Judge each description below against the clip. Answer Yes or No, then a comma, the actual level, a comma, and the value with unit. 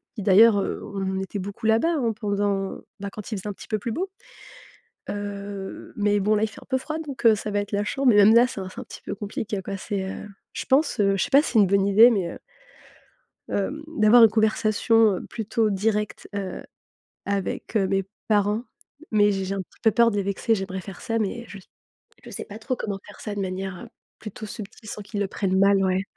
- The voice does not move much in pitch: Yes, narrow, 2.2 semitones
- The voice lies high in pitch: Yes, high, 205 Hz